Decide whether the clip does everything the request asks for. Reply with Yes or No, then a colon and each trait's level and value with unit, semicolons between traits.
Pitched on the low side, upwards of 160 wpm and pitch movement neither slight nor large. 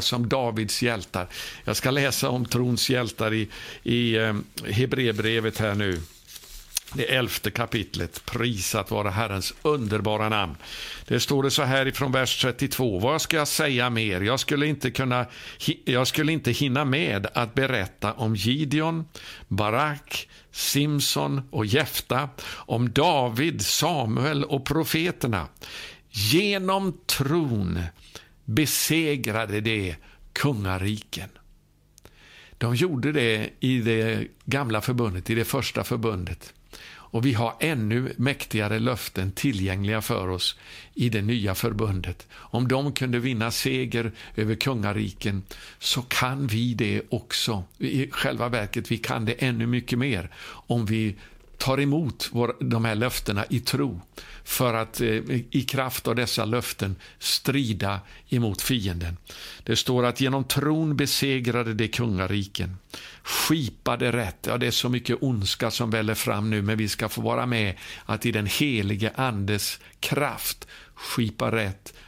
No: low, 120 Hz; average, 135 wpm; average, 3.8 semitones